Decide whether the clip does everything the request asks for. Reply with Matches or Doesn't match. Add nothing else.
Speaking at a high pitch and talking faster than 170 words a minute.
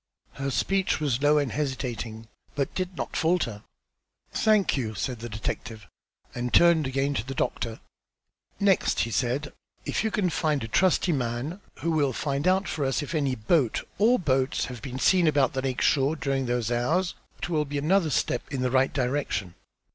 Doesn't match